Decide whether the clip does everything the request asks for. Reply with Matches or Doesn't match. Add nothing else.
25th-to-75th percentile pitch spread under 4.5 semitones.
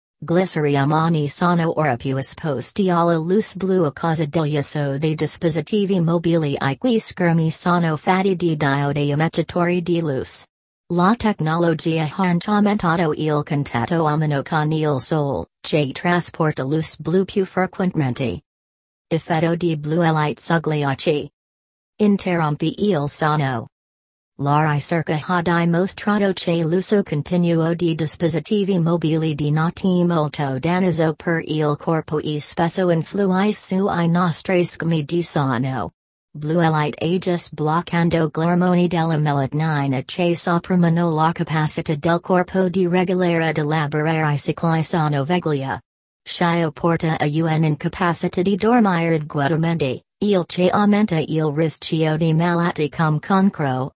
Matches